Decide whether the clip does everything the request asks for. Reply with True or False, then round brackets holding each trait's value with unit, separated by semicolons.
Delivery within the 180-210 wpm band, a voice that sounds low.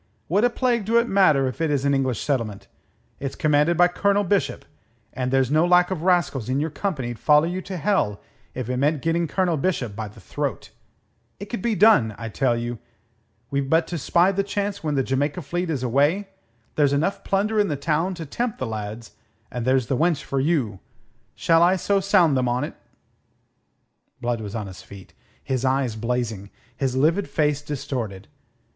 False (190 wpm; 145 Hz)